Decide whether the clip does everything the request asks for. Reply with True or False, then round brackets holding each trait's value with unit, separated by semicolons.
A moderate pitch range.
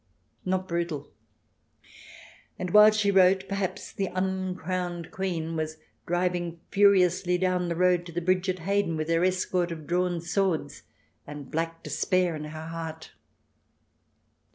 False (2.0 semitones)